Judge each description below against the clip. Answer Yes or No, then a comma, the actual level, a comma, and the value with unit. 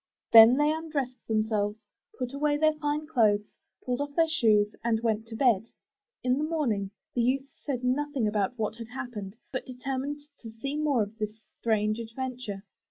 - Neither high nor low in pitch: No, high, 245 Hz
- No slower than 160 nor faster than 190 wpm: Yes, average, 170 wpm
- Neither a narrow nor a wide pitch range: Yes, average, 4.5 semitones